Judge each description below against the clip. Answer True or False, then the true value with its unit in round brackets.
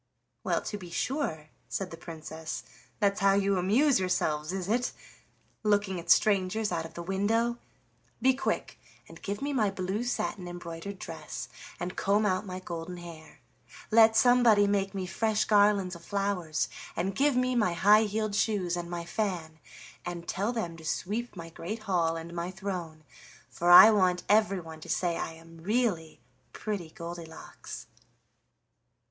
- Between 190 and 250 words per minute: False (160 wpm)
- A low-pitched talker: False (190 Hz)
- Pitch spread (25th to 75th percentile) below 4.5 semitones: True (3.8 semitones)